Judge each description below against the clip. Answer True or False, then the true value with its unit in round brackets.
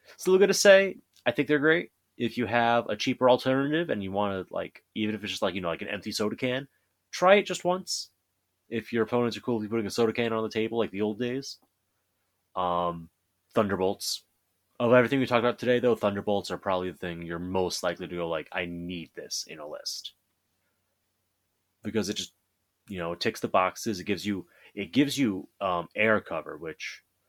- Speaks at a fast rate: True (210 wpm)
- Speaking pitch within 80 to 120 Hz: True (105 Hz)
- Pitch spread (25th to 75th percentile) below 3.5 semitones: False (4.6 semitones)